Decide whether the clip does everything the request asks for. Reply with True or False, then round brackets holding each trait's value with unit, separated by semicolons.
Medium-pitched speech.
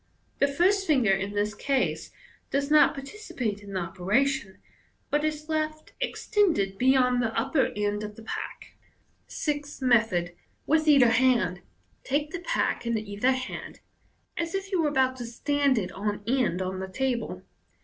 False (255 Hz)